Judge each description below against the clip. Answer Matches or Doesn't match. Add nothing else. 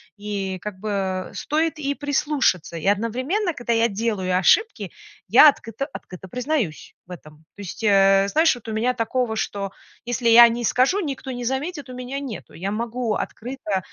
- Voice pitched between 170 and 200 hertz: Doesn't match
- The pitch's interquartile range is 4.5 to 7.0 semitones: Matches